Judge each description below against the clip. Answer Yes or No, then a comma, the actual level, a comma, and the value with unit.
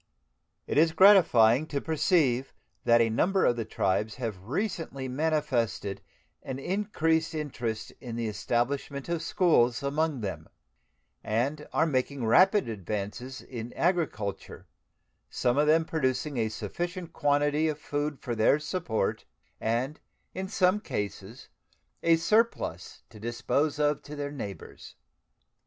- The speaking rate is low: Yes, slow, 130 wpm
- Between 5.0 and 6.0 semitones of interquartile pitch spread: Yes, wide, 5.5 semitones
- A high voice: No, medium, 140 Hz